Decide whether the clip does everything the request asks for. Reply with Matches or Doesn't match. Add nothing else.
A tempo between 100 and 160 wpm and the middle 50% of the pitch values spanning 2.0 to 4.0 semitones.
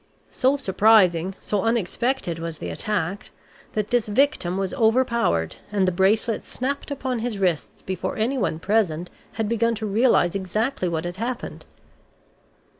Doesn't match